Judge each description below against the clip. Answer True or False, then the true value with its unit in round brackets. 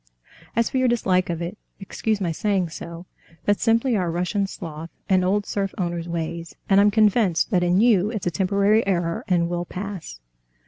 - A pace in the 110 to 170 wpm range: False (185 wpm)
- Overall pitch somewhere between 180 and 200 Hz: True (185 Hz)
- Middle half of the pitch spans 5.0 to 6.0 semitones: False (3.2 semitones)